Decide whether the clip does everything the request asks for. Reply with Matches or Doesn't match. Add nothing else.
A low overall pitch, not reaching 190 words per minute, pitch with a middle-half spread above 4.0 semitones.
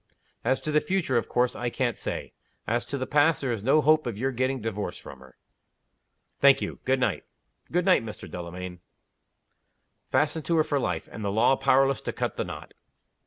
Doesn't match